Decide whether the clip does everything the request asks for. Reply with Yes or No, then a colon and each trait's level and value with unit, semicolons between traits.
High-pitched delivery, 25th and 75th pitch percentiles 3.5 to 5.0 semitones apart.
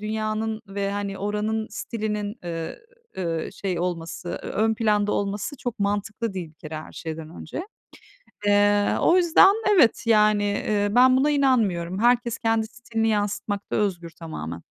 No: high, 210 Hz; narrow, 2.4 semitones